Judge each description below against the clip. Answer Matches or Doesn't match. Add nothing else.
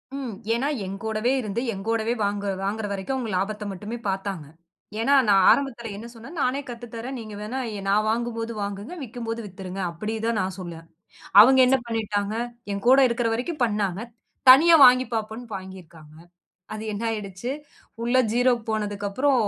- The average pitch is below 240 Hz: Matches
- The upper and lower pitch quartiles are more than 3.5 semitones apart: Doesn't match